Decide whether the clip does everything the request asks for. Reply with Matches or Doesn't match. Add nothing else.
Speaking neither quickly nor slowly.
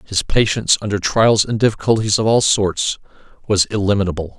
Matches